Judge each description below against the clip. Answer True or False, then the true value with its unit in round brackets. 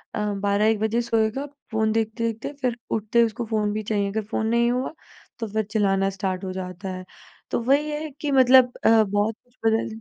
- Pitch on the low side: False (220 Hz)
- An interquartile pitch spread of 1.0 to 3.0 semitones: True (2.6 semitones)